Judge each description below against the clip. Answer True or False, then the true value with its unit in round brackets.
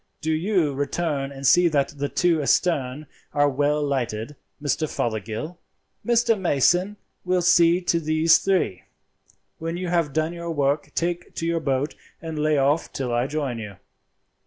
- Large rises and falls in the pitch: False (3.6 semitones)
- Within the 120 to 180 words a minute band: True (160 wpm)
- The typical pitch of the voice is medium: True (155 Hz)